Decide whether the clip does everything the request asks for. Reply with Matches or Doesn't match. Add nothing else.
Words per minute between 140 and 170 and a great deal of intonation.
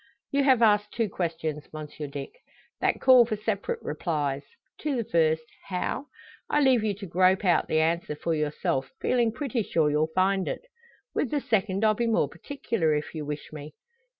Doesn't match